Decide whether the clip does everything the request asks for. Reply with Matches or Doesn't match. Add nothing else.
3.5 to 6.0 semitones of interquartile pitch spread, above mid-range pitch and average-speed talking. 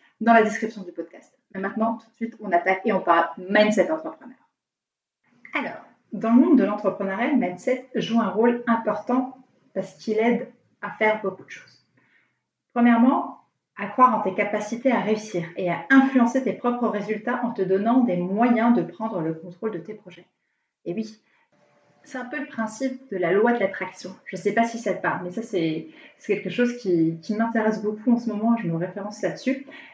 Matches